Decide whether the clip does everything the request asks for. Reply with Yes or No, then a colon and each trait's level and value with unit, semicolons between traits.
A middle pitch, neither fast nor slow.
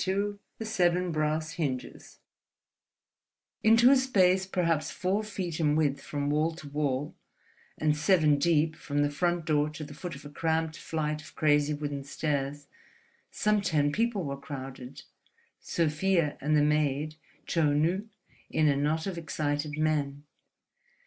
Yes: medium, 155 Hz; average, 150 wpm